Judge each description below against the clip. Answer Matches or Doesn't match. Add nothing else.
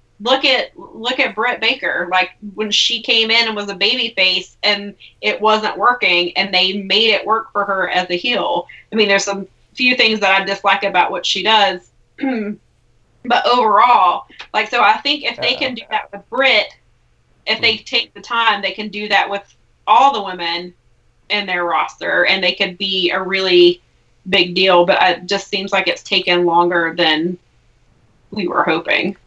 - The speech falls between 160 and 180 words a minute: Doesn't match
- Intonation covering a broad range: Doesn't match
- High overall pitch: Matches